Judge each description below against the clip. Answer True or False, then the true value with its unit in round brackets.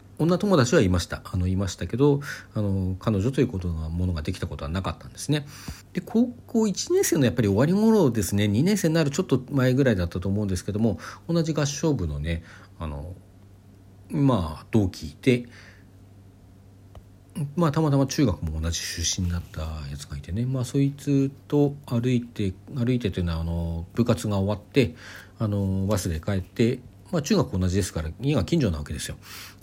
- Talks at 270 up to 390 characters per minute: True (300 characters per minute)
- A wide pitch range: True (6.8 semitones)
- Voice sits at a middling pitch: False (100 Hz)